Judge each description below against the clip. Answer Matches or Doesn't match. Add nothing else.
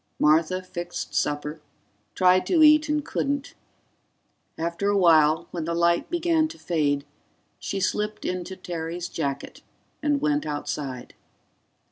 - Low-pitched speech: Doesn't match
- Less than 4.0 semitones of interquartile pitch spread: Doesn't match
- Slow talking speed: Matches